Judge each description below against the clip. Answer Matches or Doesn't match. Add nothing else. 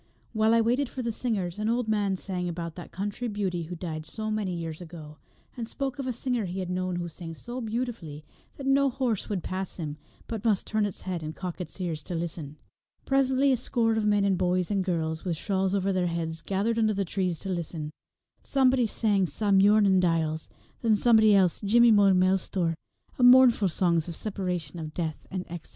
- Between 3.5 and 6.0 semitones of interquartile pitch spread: Matches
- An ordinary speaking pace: Doesn't match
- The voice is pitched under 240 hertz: Matches